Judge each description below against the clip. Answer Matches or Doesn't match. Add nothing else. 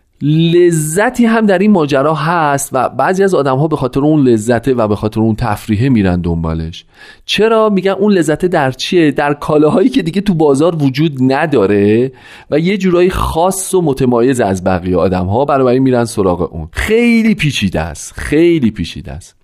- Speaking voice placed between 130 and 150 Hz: Matches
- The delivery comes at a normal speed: Doesn't match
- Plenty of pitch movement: Matches